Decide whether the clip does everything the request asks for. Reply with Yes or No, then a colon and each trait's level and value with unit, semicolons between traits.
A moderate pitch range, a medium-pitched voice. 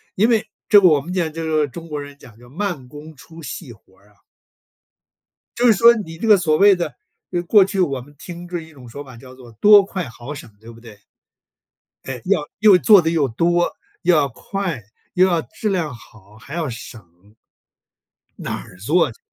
No: wide, 6.5 semitones; medium, 160 Hz